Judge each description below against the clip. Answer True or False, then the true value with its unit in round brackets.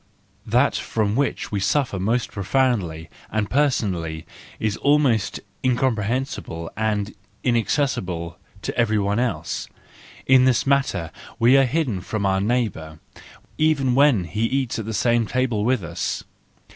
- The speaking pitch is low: True (115 Hz)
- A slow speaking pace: True (130 wpm)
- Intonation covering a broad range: False (4.7 semitones)